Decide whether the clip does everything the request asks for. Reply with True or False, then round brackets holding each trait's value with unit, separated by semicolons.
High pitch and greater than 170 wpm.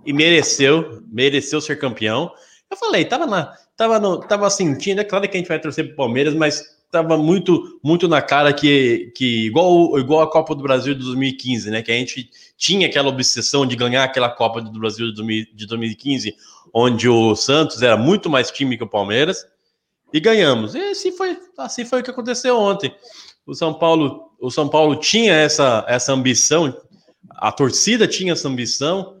False (150 Hz; 185 wpm)